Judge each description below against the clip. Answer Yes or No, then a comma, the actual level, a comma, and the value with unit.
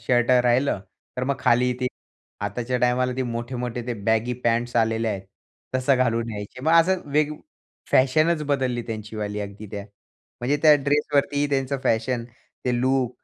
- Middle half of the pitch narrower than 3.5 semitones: Yes, average, 2.8 semitones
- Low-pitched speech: Yes, low, 125 Hz